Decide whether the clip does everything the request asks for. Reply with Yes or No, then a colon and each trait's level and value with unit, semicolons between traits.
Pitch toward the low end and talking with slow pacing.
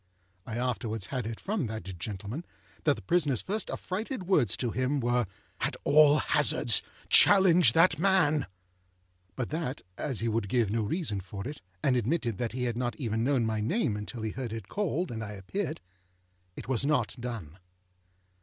No: low, 125 Hz; average, 175 wpm